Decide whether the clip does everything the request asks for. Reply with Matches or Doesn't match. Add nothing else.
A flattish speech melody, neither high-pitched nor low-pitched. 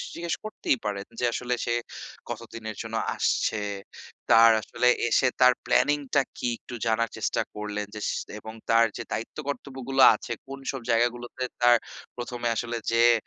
Doesn't match